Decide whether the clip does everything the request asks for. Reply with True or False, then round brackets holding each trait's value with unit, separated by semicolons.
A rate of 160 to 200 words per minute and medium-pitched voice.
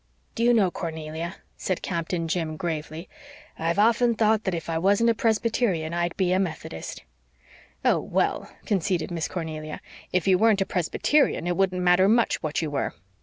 True (170 wpm; 180 Hz)